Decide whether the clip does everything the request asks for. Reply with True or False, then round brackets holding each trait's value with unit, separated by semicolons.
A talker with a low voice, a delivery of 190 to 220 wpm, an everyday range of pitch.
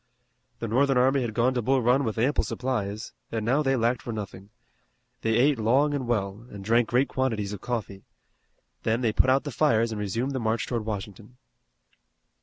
True (115 Hz; 195 wpm; 3.2 semitones)